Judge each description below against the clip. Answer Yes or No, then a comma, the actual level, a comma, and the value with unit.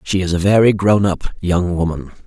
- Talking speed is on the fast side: Yes, fast, 210 wpm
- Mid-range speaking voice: No, very low, 95 Hz